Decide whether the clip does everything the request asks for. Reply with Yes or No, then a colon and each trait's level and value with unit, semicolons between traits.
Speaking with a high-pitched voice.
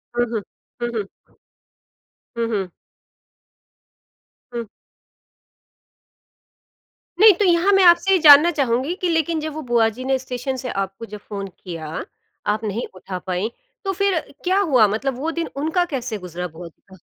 Yes: very high, 250 Hz